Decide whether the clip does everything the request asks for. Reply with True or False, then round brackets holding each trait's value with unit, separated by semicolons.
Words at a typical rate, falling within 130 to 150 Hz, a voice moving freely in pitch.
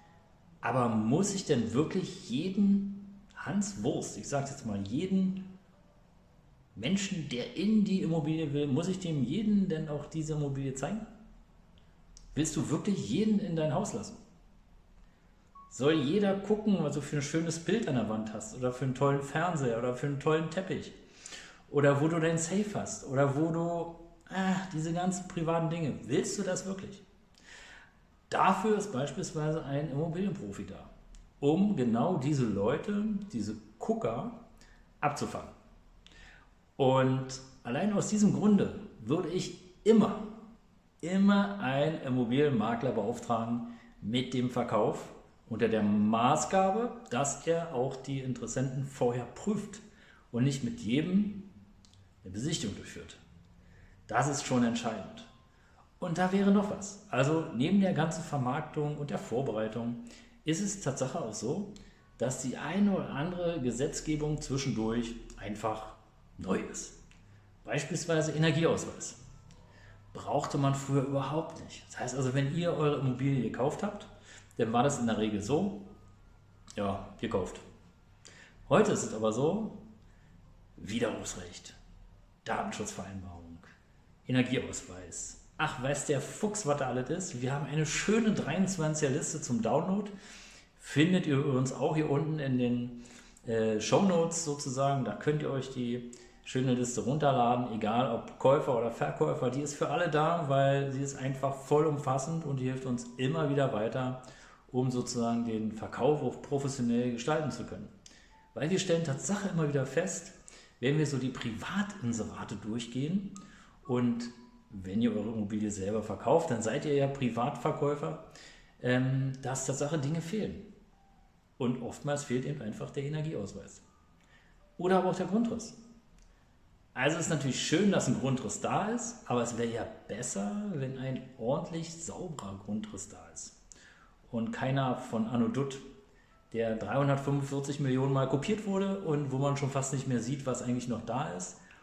True (145 wpm; 140 Hz; 6.2 semitones)